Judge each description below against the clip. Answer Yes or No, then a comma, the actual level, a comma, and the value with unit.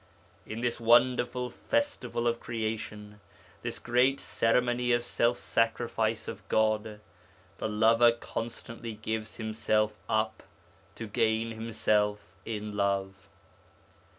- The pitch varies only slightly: Yes, narrow, 1.7 semitones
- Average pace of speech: No, slow, 105 wpm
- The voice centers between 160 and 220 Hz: No, low, 115 Hz